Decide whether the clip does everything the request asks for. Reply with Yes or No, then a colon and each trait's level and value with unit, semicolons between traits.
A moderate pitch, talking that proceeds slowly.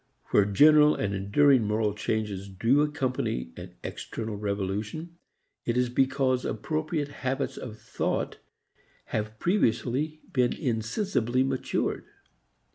No: low, 125 Hz; slow, 110 wpm